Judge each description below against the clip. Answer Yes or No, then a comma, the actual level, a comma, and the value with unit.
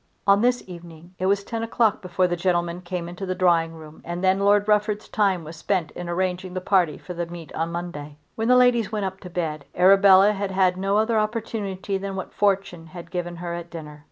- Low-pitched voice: No, medium, 185 Hz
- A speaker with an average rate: No, fast, 220 wpm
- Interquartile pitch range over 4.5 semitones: No, average, 2.7 semitones